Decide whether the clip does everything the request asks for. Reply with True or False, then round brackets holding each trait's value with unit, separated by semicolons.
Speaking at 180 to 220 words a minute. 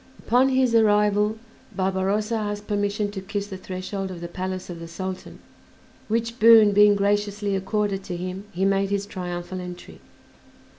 False (155 wpm)